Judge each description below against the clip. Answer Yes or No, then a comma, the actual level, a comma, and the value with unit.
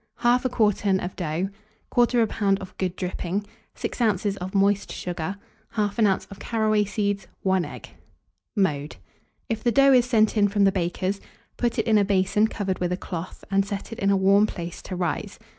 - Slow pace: No, average, 190 wpm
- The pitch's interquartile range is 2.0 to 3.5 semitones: Yes, narrow, 2.4 semitones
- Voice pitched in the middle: No, high, 200 Hz